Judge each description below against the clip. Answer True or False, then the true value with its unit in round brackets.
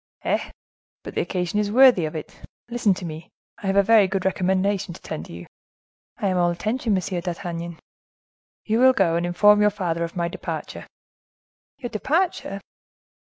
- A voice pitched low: False (190 Hz)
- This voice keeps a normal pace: True (170 wpm)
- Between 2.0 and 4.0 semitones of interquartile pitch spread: True (3.3 semitones)